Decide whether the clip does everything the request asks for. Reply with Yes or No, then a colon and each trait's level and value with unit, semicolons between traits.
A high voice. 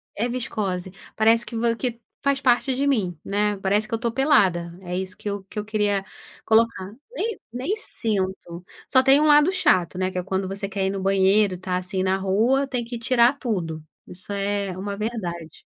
Yes: high, 205 Hz